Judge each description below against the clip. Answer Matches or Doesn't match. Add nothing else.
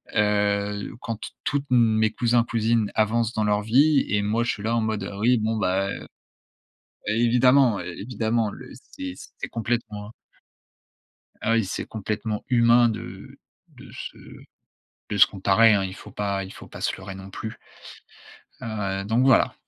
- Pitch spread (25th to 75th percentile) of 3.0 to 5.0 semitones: Doesn't match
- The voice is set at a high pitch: Doesn't match